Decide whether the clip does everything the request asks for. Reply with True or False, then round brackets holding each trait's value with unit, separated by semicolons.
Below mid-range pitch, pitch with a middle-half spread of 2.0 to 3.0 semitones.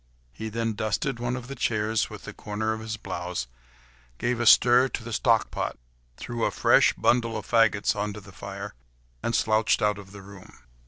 True (110 Hz; 2.4 semitones)